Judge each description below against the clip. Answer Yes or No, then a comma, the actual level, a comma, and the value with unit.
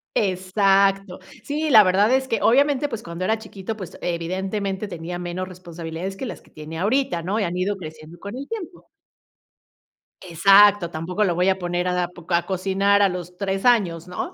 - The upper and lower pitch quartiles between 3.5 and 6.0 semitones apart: No, average, 2.9 semitones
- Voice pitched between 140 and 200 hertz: Yes, high, 190 Hz